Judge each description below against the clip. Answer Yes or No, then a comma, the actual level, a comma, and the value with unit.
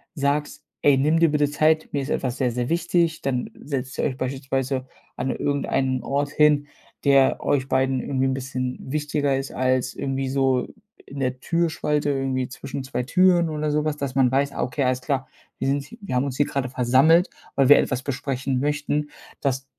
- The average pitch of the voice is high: No, low, 135 Hz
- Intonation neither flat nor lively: No, narrow, 2.2 semitones